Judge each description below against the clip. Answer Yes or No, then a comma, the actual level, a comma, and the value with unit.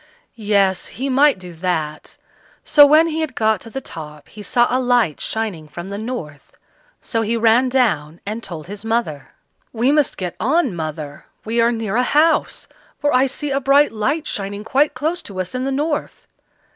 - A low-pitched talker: No, high, 225 Hz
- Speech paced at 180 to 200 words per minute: Yes, average, 190 wpm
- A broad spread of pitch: Yes, wide, 6.3 semitones